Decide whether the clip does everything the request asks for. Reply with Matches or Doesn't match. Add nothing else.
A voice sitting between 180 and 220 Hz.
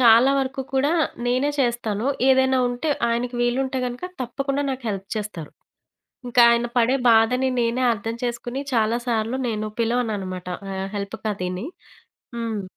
Doesn't match